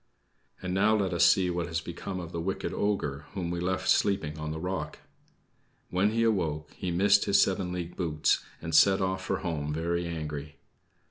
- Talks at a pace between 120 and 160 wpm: No, average, 190 wpm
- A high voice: No, very low, 85 Hz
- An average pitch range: Yes, average, 3.1 semitones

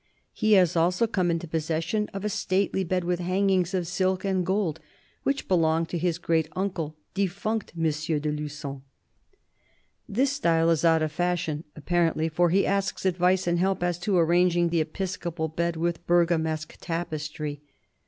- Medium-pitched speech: Yes, medium, 175 Hz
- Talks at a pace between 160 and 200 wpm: Yes, average, 165 wpm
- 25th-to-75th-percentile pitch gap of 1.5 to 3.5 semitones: Yes, narrow, 2.6 semitones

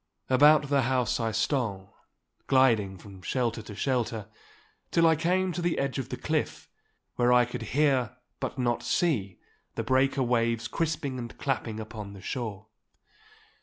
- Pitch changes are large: No, average, 3.7 semitones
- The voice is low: Yes, low, 125 Hz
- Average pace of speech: Yes, average, 155 wpm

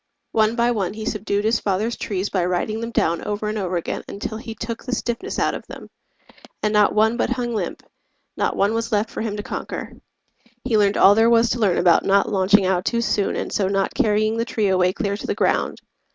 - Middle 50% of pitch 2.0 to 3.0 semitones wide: Yes, narrow, 2.6 semitones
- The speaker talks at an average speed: No, fast, 230 wpm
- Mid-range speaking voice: No, high, 210 Hz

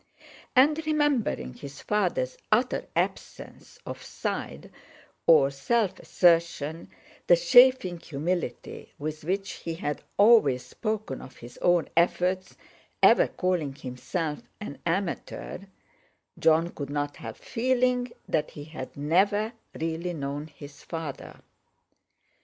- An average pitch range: No, wide, 6.5 semitones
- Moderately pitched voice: Yes, medium, 170 Hz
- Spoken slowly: Yes, slow, 110 wpm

